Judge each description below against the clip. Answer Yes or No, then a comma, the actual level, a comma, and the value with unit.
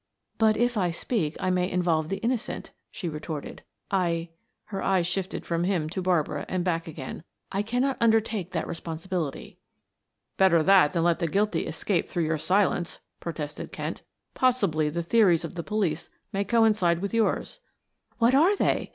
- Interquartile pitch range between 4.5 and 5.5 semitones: No, average, 4.1 semitones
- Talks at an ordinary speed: Yes, average, 170 wpm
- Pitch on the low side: No, medium, 180 Hz